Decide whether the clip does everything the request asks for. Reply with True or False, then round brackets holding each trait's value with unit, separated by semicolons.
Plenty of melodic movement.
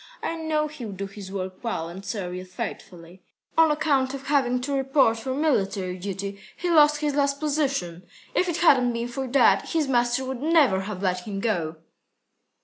True (7.0 semitones)